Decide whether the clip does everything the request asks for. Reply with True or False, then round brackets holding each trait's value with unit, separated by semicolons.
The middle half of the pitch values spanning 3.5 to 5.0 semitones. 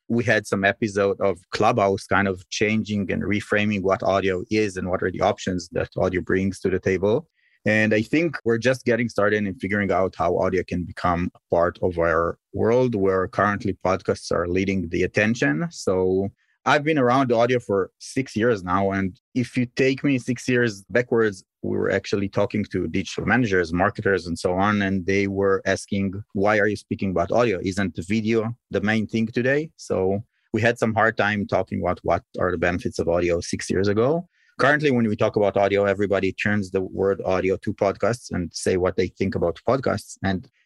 False (3.0 semitones)